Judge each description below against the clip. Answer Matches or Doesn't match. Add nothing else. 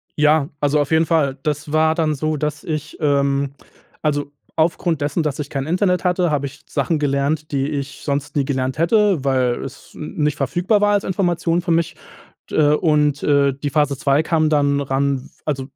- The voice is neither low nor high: Matches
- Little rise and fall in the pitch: Matches